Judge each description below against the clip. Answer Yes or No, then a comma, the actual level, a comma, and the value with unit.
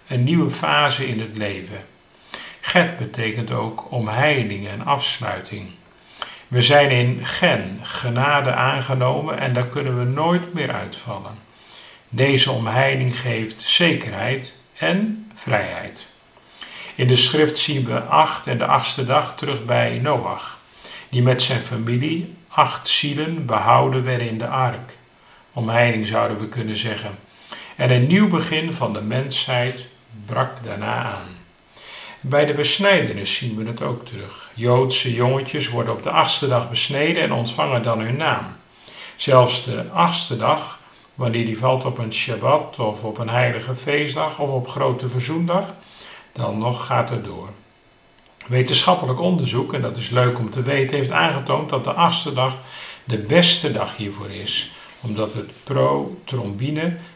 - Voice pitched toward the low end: Yes, low, 125 Hz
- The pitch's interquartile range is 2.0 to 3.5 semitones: No, average, 4.0 semitones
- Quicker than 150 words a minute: No, average, 145 wpm